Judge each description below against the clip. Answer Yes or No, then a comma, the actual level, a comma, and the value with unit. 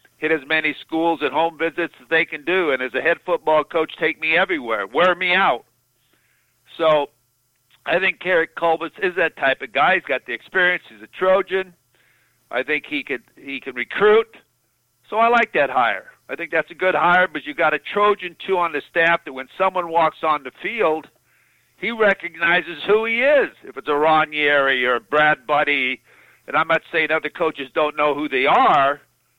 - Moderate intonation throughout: Yes, average, 3.5 semitones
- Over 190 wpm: Yes, average, 200 wpm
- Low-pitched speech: No, medium, 165 Hz